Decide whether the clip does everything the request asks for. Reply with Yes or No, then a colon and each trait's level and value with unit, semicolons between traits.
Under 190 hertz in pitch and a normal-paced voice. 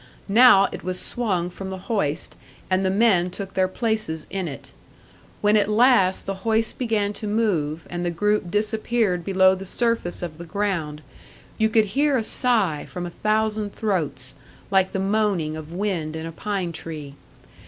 No: high, 195 Hz; average, 175 wpm